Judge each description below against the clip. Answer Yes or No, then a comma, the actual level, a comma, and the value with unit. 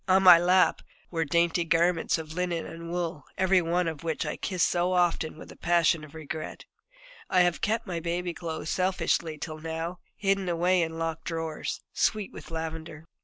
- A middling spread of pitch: No, narrow, 1.8 semitones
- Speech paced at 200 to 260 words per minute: No, average, 185 wpm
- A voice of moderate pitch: Yes, medium, 170 Hz